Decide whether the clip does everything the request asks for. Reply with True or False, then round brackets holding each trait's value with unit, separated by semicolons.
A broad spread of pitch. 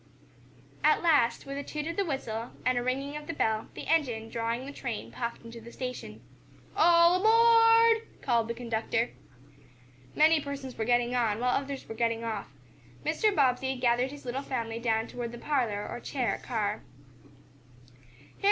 False (4.2 semitones)